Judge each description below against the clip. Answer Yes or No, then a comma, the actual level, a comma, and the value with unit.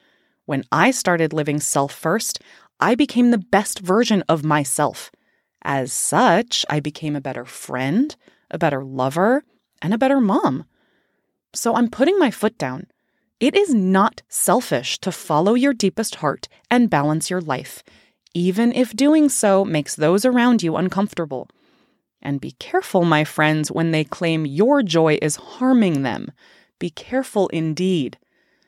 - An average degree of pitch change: No, wide, 7.6 semitones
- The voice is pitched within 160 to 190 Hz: Yes, medium, 185 Hz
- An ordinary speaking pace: Yes, average, 150 wpm